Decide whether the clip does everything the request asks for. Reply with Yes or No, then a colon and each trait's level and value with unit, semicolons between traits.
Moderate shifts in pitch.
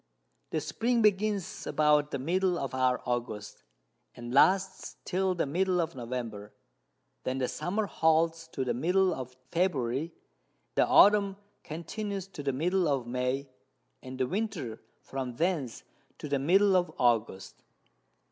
No: wide, 6.6 semitones